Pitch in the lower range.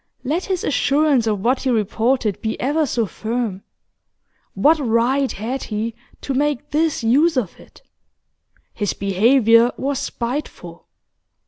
No: very high, 250 Hz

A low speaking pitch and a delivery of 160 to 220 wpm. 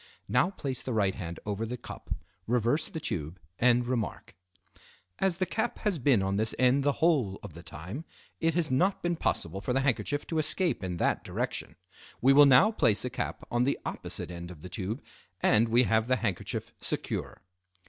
Yes: low, 125 Hz; average, 195 wpm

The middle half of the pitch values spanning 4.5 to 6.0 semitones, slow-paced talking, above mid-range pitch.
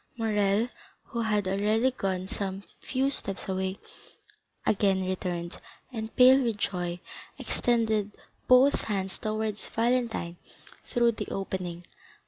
No: average, 3.4 semitones; slow, 110 wpm; high, 210 Hz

